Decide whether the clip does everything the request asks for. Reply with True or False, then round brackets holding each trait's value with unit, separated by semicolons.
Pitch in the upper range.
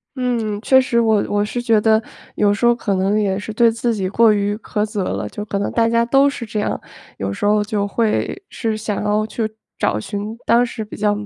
True (215 Hz)